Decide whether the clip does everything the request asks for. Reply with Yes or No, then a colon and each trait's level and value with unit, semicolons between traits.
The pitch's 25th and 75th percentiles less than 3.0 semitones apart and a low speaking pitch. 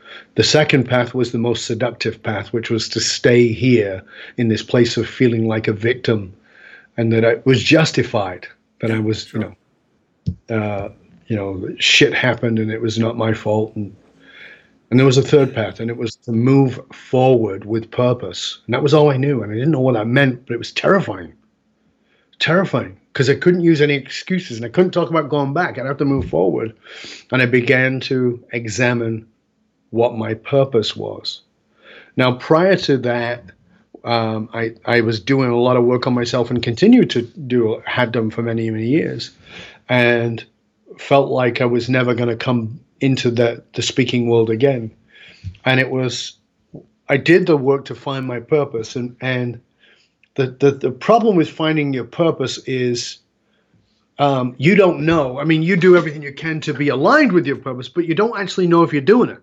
No: average, 3.4 semitones; low, 125 Hz